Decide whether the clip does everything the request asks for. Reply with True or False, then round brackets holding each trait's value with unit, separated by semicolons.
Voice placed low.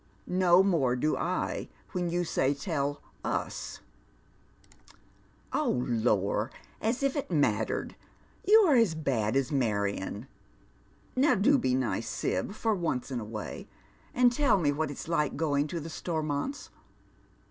False (155 Hz)